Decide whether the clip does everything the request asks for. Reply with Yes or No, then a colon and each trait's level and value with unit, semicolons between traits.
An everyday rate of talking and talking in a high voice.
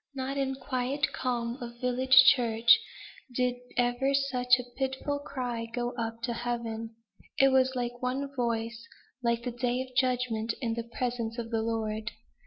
Yes: average, 160 wpm; high, 245 Hz